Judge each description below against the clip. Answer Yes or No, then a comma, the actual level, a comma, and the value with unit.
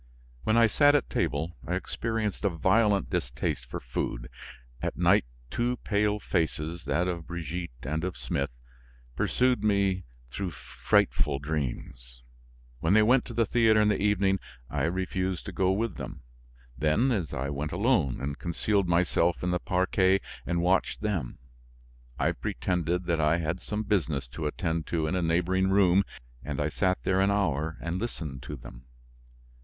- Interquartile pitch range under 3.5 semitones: No, average, 4.5 semitones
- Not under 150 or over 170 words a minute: Yes, average, 160 wpm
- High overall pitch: No, very low, 90 Hz